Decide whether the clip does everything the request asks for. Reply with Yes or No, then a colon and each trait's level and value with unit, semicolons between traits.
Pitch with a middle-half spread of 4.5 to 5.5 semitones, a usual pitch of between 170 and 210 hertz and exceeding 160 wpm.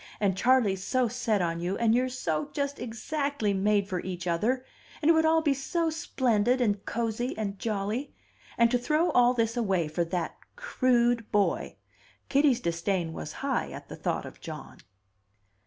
No: average, 4.8 semitones; high, 230 Hz; average, 170 wpm